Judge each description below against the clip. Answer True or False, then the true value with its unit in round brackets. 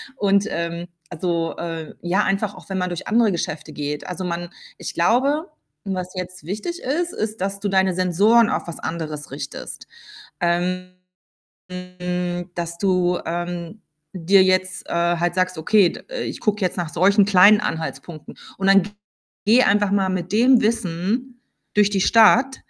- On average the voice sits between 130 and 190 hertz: True (185 Hz)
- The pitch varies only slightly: False (3.1 semitones)